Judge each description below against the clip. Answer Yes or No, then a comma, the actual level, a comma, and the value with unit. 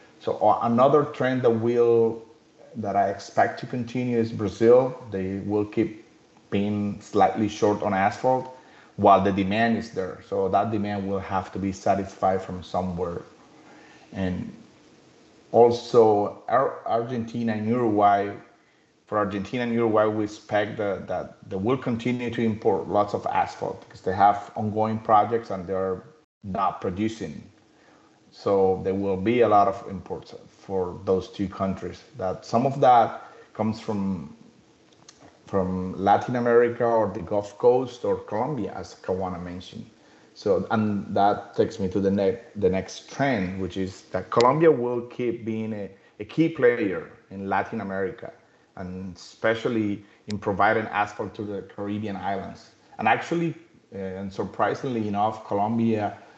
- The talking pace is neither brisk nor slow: Yes, average, 145 wpm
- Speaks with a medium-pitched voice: No, low, 105 Hz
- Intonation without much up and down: No, average, 3.0 semitones